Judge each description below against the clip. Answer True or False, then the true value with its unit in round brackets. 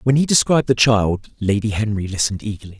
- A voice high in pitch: False (110 Hz)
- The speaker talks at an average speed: True (195 wpm)